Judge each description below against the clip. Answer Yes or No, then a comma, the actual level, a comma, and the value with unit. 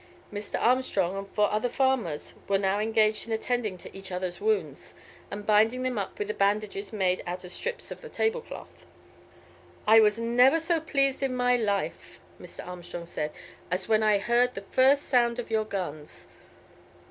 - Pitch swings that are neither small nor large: Yes, average, 4.2 semitones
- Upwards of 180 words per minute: No, average, 175 wpm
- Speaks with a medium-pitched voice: No, high, 215 Hz